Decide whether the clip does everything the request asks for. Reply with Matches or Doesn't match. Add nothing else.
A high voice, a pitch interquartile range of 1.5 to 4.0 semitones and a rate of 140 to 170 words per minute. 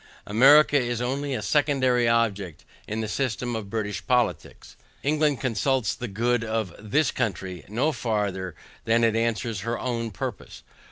Doesn't match